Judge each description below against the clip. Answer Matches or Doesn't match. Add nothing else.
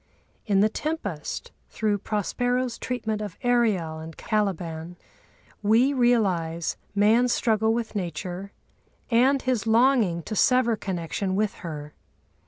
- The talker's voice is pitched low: Doesn't match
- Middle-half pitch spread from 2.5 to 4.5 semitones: Doesn't match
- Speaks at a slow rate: Matches